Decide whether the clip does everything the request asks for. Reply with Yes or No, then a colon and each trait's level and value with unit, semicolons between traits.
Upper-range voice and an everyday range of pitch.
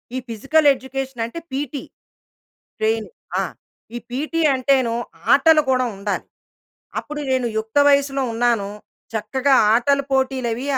Yes: very high, 265 Hz; average, 3.1 semitones